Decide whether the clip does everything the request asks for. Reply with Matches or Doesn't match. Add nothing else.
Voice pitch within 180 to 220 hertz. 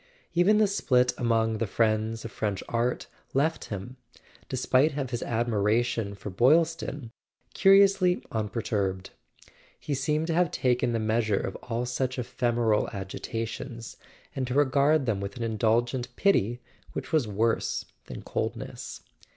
Doesn't match